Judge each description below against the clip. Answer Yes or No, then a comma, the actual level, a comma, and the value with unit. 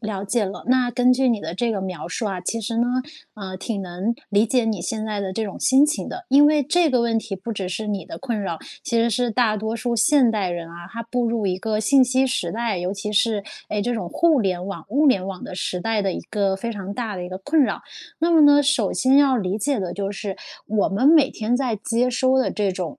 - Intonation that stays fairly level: No, average, 4.4 semitones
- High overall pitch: Yes, high, 220 Hz